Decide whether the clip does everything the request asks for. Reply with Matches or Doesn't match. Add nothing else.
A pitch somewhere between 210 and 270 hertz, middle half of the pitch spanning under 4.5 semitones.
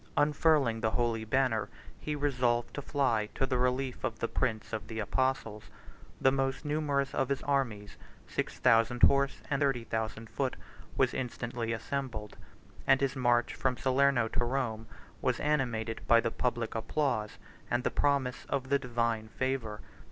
Doesn't match